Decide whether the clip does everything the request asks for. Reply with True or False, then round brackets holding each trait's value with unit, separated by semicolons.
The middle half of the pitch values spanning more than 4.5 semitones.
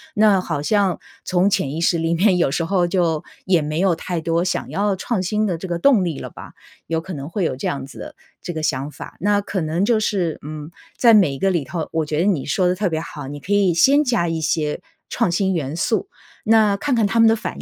False (4.2 semitones)